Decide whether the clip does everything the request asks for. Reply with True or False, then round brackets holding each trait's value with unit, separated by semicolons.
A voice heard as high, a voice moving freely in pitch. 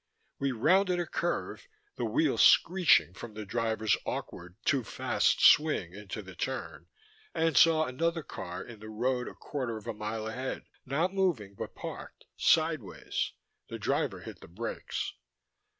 False (125 Hz; 6.9 semitones)